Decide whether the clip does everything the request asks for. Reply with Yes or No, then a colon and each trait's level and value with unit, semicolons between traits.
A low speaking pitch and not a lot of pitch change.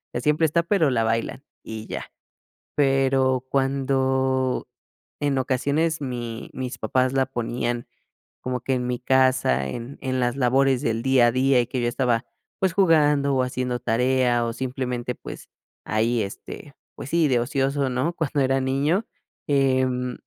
Yes: low, 130 Hz; narrow, 1.9 semitones